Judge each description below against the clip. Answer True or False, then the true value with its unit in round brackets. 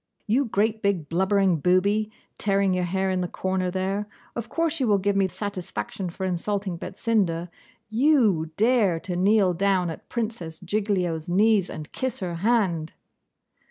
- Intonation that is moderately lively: True (3.0 semitones)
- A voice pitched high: True (195 Hz)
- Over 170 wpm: False (155 wpm)